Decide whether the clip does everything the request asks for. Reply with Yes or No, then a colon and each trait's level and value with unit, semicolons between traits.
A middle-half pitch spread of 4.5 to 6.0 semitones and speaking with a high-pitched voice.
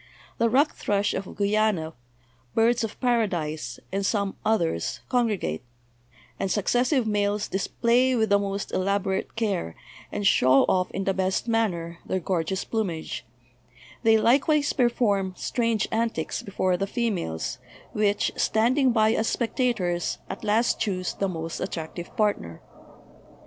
No: average, 3.8 semitones; high, 205 Hz